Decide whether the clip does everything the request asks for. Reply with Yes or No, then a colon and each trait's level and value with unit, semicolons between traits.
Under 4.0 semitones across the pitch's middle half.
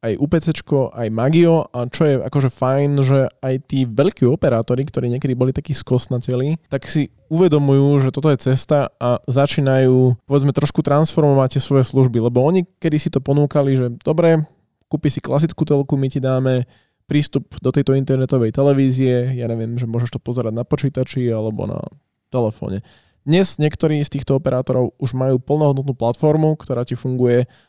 Yes: average, 2.7 semitones